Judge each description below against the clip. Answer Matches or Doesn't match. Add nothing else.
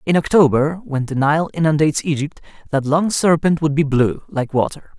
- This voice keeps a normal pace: Matches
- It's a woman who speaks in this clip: Doesn't match